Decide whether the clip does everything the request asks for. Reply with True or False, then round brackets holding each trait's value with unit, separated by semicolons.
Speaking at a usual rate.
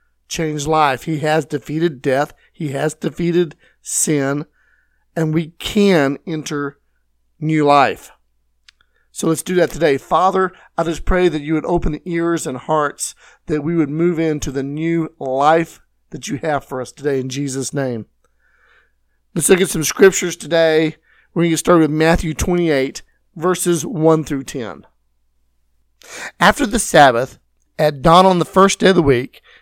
True (160 wpm)